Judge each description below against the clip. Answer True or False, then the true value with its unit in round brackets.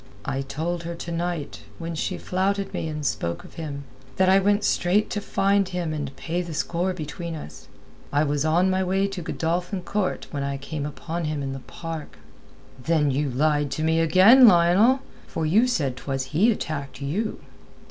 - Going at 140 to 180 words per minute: False (190 wpm)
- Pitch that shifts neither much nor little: True (4.1 semitones)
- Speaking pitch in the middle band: True (165 Hz)